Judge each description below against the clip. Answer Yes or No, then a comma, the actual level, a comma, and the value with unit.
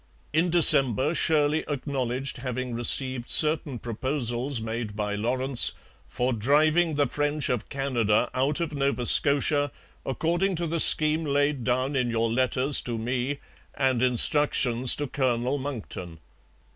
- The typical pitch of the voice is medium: No, low, 130 Hz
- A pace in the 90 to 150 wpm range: Yes, slow, 135 wpm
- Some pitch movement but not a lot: Yes, average, 3.3 semitones